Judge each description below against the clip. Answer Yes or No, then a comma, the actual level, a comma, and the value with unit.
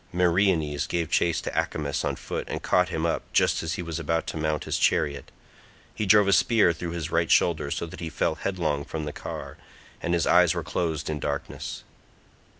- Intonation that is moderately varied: No, narrow, 2.1 semitones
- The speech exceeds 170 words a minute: Yes, fast, 205 wpm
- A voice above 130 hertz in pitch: No, very low, 85 Hz